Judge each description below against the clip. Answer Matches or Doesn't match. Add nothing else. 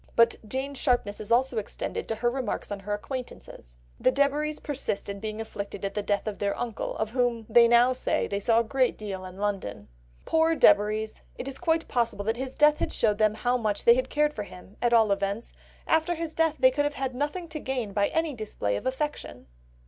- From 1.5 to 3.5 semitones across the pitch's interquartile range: Doesn't match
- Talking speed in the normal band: Doesn't match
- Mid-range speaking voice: Doesn't match